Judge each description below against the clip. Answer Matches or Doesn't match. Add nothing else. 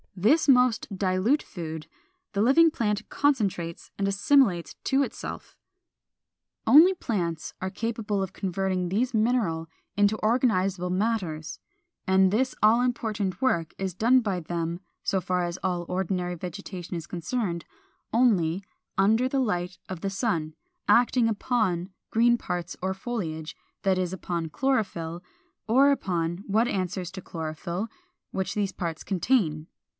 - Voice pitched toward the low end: Doesn't match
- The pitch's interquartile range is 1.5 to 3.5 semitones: Doesn't match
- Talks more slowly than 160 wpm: Matches